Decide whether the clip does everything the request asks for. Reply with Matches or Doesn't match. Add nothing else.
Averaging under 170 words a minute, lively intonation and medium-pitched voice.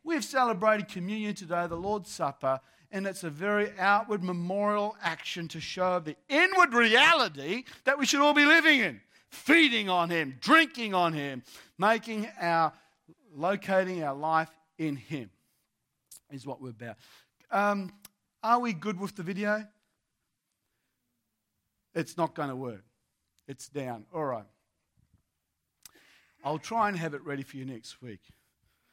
Matches